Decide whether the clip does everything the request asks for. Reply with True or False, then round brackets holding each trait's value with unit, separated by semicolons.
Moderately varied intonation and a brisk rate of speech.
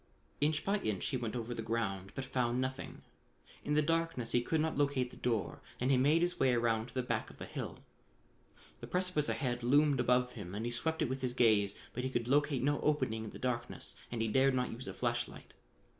True (3.6 semitones; 230 wpm)